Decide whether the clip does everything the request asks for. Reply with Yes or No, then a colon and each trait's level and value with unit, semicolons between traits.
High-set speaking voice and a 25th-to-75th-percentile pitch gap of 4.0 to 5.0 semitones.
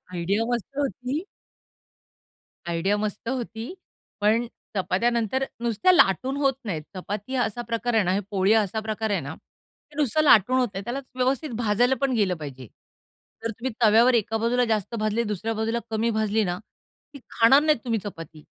No: high, 225 Hz; average, 3.4 semitones